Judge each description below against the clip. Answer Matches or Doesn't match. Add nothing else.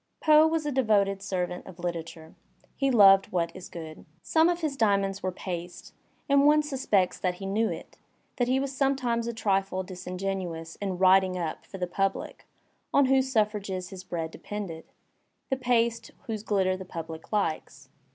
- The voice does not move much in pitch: Doesn't match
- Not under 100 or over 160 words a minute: Doesn't match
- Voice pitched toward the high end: Matches